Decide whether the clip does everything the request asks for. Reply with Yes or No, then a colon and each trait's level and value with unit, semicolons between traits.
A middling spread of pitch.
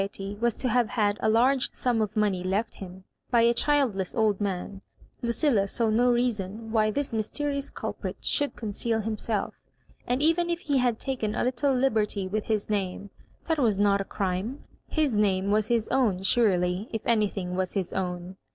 Yes: average, 3.8 semitones